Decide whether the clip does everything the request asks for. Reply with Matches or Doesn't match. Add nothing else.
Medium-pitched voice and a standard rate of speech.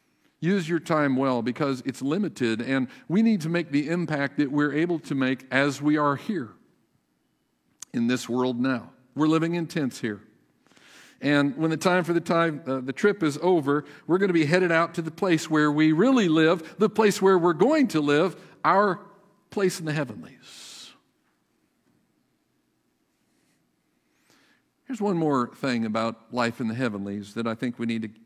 Matches